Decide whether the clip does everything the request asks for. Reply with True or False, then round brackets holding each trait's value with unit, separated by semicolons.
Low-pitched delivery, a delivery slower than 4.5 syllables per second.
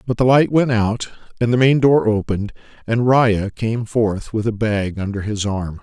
False (110 Hz; 4.6 syllables/s)